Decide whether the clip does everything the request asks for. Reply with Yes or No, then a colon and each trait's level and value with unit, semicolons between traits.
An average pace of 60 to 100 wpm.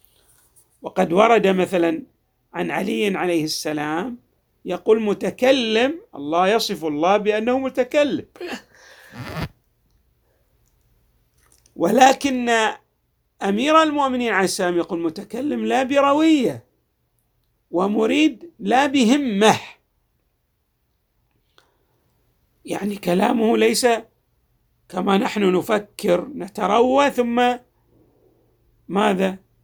Yes: average, 70 wpm